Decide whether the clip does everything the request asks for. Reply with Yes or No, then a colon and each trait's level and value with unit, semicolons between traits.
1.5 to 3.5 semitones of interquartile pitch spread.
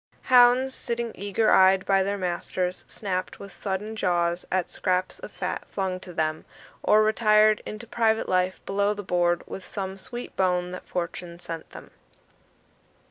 Yes: average, 2.9 semitones